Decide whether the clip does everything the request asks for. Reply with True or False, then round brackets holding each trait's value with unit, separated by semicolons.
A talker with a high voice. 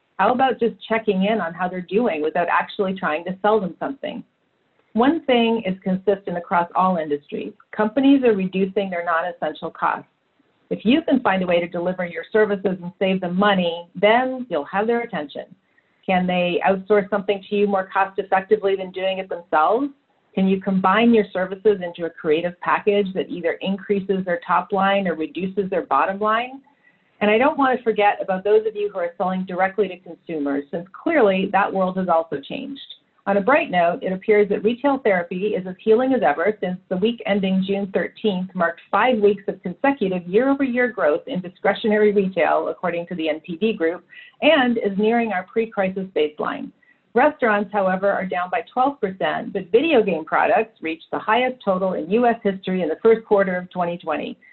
True (195 Hz)